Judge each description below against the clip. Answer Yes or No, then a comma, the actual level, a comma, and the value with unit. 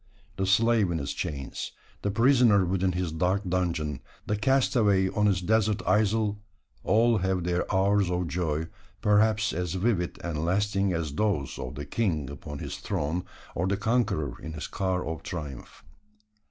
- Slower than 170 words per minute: Yes, average, 160 wpm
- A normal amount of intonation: Yes, average, 4.1 semitones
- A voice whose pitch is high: No, very low, 95 Hz